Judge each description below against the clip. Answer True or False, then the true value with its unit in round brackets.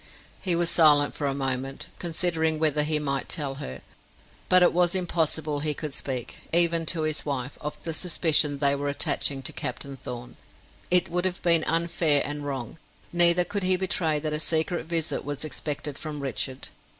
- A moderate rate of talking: True (180 wpm)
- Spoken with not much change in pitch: False (3.1 semitones)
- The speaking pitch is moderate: True (155 Hz)